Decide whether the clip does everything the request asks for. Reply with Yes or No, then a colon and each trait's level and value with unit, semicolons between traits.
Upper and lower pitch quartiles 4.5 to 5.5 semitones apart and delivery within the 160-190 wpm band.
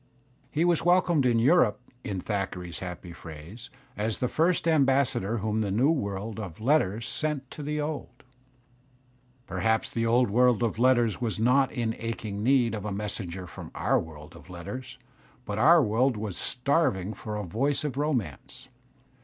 Yes: average, 5.2 semitones; average, 165 wpm